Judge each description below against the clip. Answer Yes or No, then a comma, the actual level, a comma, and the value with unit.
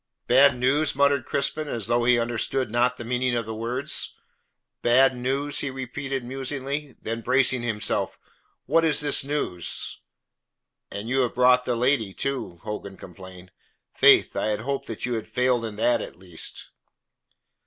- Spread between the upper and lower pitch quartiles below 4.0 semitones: Yes, average, 2.9 semitones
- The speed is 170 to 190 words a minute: No, average, 160 wpm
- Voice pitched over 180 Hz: No, low, 125 Hz